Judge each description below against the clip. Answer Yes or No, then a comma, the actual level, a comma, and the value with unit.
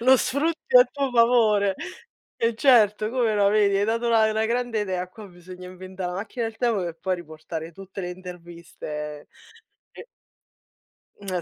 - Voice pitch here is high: Yes, high, 205 Hz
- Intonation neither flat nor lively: Yes, average, 4.3 semitones